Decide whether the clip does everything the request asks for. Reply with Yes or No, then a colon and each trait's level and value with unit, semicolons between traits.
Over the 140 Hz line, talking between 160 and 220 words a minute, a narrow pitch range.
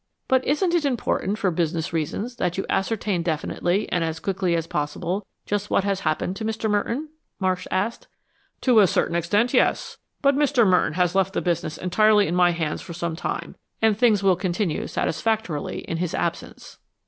No: high, 190 Hz; average, 185 wpm; average, 4.2 semitones